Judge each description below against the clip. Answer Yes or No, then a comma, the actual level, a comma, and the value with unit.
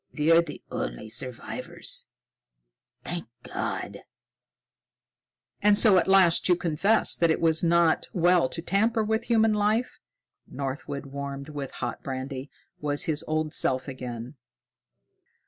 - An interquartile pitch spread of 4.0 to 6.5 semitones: Yes, average, 5.1 semitones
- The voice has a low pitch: No, medium, 160 Hz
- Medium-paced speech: No, slow, 125 wpm